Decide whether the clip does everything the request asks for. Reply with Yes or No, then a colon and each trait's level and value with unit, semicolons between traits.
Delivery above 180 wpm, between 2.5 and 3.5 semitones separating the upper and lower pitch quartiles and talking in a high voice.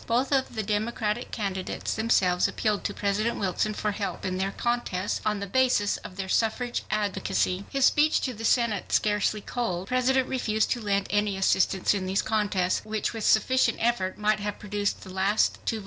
Yes: average, 190 wpm; average, 2.9 semitones; high, 210 Hz